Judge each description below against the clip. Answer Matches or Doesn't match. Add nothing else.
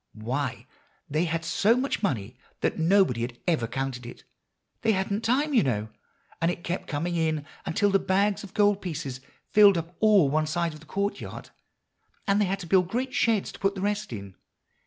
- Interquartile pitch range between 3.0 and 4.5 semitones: Doesn't match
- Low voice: Doesn't match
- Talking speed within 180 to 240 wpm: Matches